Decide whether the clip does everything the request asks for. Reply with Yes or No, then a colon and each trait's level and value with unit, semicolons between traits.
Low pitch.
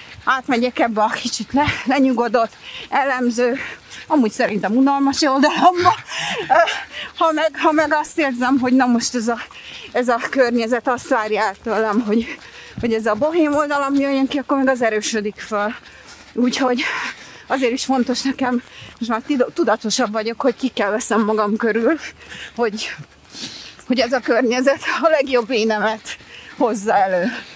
No: very high, 250 Hz